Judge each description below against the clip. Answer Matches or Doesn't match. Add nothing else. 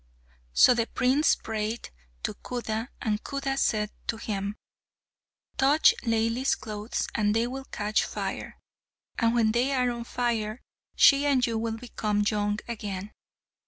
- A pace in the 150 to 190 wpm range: Doesn't match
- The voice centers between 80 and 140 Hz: Doesn't match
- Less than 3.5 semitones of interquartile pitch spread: Matches